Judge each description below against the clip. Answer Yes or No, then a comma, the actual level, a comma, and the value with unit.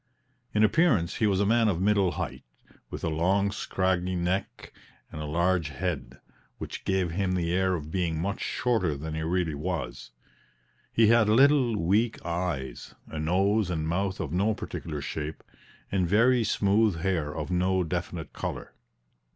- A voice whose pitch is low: Yes, very low, 90 Hz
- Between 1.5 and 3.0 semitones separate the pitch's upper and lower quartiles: No, average, 3.7 semitones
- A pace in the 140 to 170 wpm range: Yes, average, 160 wpm